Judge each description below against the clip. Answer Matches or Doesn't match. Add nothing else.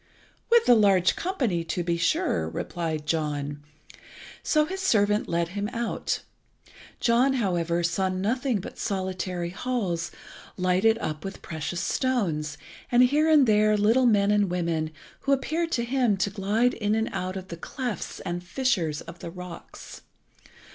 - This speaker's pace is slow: Doesn't match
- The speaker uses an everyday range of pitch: Doesn't match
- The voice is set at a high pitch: Matches